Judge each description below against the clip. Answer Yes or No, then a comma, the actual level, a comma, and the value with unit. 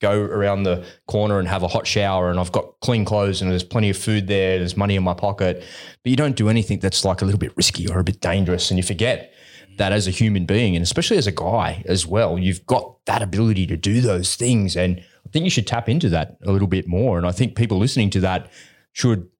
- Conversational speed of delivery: No, fast, 255 wpm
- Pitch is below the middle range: Yes, low, 100 Hz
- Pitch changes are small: No, average, 3.2 semitones